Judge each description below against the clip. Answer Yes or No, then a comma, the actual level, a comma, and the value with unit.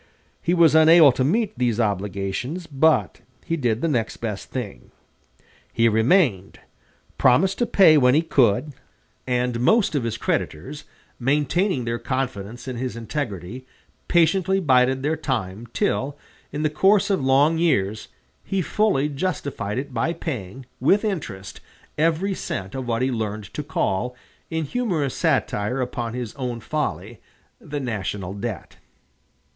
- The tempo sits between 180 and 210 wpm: No, average, 140 wpm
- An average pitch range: No, wide, 5.7 semitones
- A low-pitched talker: Yes, low, 130 Hz